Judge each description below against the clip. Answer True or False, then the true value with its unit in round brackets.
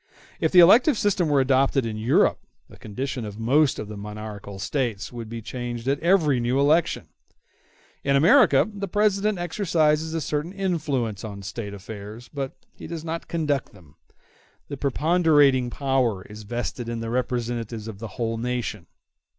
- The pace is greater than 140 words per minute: True (160 wpm)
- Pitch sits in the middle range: False (130 Hz)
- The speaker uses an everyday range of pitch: False (5.8 semitones)